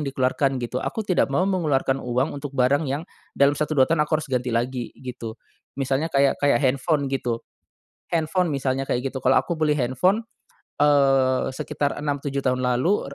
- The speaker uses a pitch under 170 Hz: Yes, low, 135 Hz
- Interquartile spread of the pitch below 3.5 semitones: Yes, narrow, 2.6 semitones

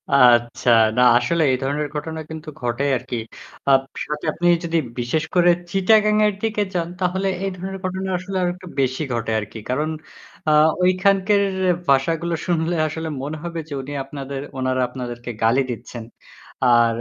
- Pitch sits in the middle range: Yes, medium, 155 Hz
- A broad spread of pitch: Yes, wide, 5.9 semitones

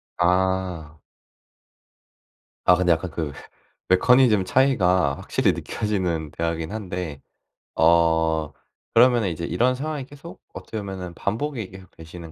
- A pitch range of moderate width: Yes, average, 4.9 semitones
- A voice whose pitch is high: No, very low, 90 Hz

